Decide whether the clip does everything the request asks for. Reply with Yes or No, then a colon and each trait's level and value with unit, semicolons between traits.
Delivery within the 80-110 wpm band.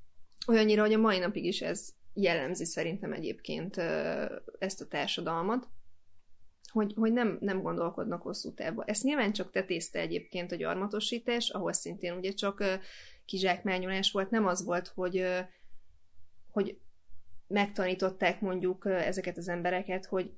No: average, 130 wpm